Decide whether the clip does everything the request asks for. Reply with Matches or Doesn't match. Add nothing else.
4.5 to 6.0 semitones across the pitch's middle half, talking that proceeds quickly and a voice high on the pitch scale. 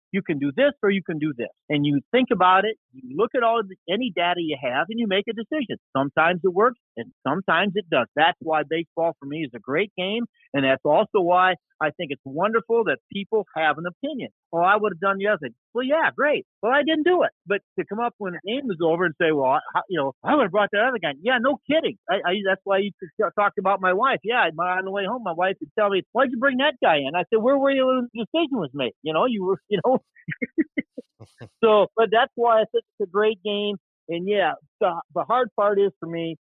Matches